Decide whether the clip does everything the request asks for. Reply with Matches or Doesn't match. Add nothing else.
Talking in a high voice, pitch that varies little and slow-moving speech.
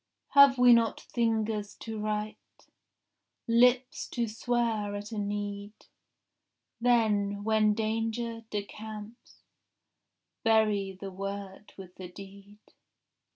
Matches